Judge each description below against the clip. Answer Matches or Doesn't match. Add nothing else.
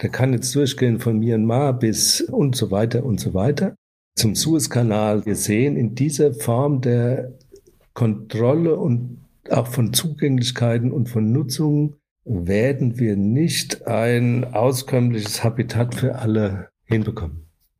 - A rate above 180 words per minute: Doesn't match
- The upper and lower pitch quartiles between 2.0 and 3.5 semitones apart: Doesn't match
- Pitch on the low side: Matches